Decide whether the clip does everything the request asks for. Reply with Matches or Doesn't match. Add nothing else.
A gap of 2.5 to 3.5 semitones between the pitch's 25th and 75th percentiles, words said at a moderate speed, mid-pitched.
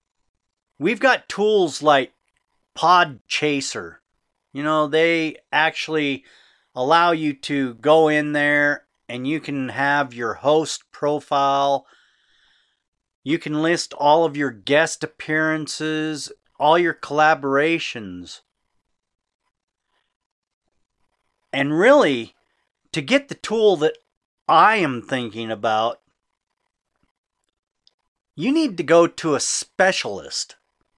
Doesn't match